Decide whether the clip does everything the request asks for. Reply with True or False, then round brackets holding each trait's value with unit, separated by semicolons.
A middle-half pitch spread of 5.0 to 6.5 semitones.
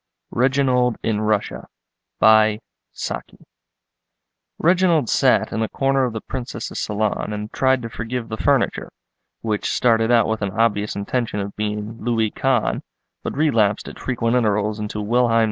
False (2.8 semitones)